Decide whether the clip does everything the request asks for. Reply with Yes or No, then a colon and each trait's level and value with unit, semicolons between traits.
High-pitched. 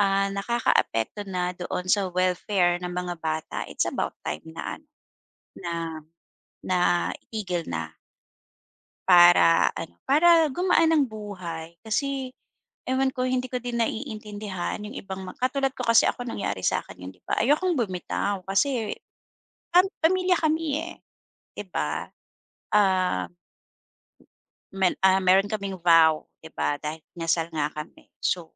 Yes: high, 195 Hz